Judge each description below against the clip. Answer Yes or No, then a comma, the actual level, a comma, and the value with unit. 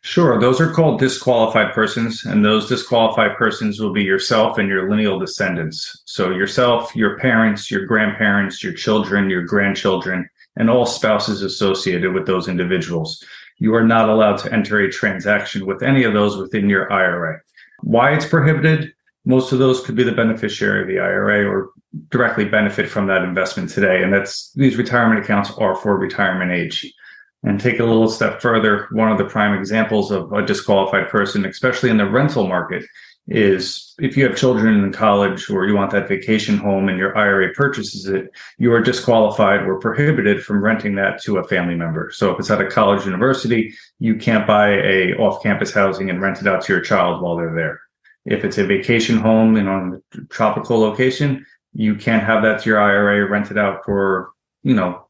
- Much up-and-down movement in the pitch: No, average, 3.4 semitones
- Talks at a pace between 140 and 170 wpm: No, average, 190 wpm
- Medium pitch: No, low, 105 Hz